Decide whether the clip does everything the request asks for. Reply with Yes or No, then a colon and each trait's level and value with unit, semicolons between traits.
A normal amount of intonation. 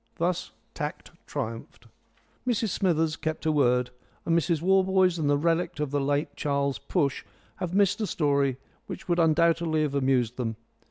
Yes: average, 3.7 semitones